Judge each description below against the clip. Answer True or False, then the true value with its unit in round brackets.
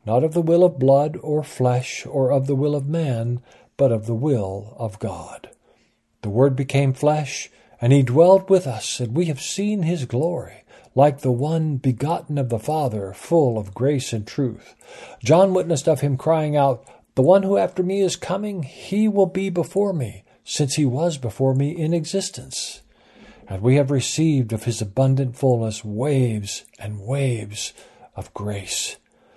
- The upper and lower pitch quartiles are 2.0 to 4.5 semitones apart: False (5.0 semitones)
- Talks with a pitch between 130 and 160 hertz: True (140 Hz)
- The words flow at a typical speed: True (175 wpm)